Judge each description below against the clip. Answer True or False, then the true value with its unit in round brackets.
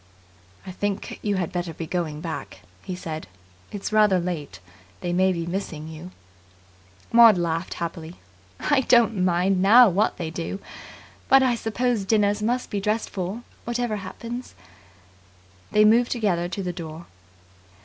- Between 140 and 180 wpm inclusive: True (150 wpm)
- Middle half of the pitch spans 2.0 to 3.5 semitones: False (4.1 semitones)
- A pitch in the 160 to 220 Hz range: True (190 Hz)